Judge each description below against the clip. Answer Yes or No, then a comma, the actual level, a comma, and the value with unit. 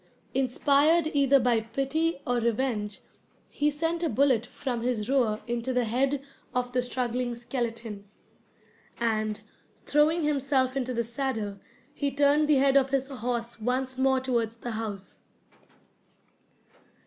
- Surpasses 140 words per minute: No, slow, 135 wpm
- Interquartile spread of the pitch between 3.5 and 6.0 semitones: No, average, 2.9 semitones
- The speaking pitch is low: No, very high, 255 Hz